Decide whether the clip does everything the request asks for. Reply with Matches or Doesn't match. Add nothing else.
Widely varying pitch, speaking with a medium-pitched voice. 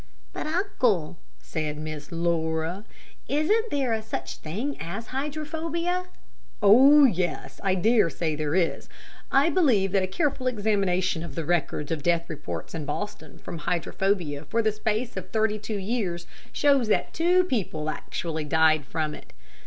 Doesn't match